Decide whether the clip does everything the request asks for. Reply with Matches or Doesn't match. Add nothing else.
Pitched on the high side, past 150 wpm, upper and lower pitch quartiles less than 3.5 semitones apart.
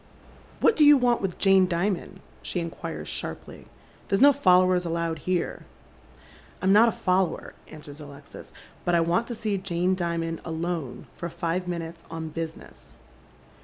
Doesn't match